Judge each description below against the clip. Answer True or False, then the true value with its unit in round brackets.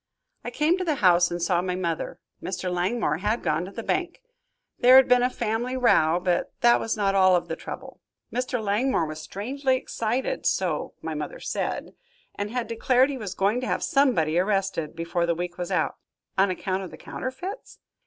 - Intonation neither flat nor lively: False (6.1 semitones)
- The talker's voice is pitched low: False (205 Hz)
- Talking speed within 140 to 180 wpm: False (195 wpm)